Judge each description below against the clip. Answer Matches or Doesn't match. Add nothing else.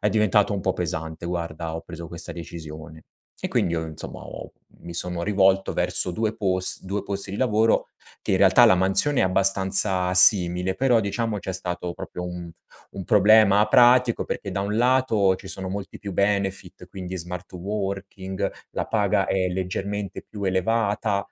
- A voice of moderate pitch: Doesn't match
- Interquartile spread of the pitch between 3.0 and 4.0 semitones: Doesn't match